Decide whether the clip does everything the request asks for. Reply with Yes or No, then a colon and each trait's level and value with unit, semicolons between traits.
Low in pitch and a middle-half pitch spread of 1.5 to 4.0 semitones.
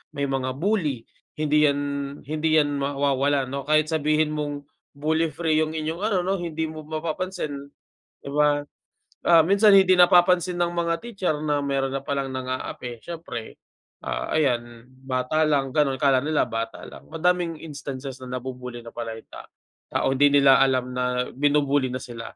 No: medium, 145 Hz; average, 3.3 semitones